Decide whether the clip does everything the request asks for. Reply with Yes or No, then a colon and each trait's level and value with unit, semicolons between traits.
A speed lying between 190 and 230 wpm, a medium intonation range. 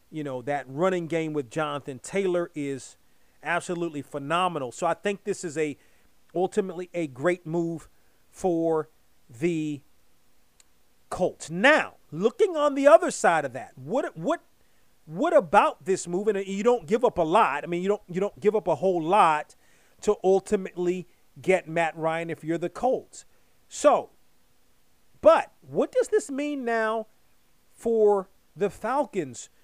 No: average, 150 wpm; average, 4.9 semitones